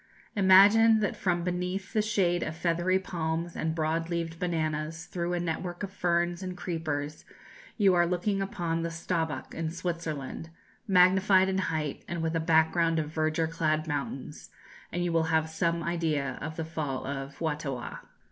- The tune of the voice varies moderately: No, narrow, 2.2 semitones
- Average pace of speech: Yes, average, 165 wpm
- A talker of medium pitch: Yes, medium, 165 Hz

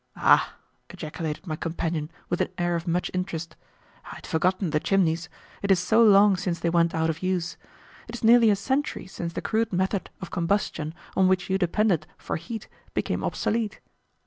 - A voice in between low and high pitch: Yes, medium, 180 Hz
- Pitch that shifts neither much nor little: Yes, average, 3.1 semitones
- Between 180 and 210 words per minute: Yes, average, 185 wpm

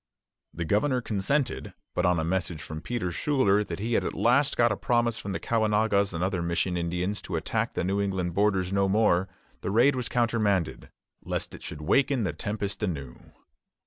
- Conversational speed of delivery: Yes, average, 190 wpm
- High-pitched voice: No, low, 100 Hz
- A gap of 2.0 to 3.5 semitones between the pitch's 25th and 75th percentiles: No, average, 4.5 semitones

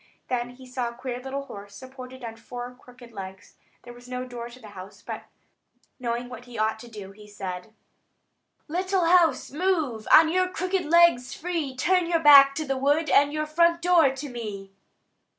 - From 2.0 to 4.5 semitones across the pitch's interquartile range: No, average, 5.1 semitones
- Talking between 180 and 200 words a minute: Yes, average, 185 wpm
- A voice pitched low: No, very high, 255 Hz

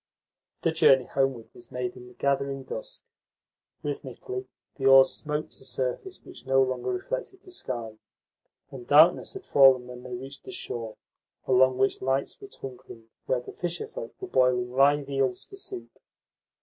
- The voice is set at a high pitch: No, low, 135 Hz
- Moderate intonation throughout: Yes, average, 3.5 semitones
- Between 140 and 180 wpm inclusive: Yes, average, 160 wpm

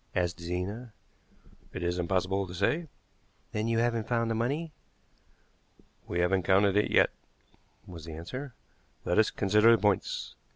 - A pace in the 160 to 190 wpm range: No, average, 150 wpm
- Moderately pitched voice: No, low, 100 Hz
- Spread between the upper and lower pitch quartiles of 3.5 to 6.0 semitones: Yes, average, 4.5 semitones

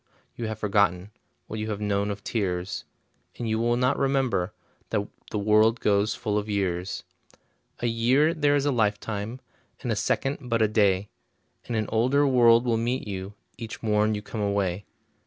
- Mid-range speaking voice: No, low, 110 Hz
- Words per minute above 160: Yes, average, 175 wpm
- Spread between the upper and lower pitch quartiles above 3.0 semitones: No, average, 2.7 semitones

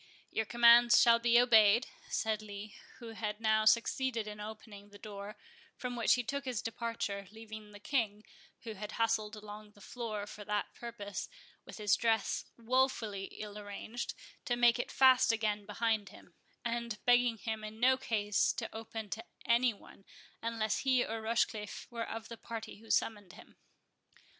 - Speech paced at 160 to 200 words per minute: Yes, average, 165 wpm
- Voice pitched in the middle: No, high, 220 Hz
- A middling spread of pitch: No, narrow, 2.1 semitones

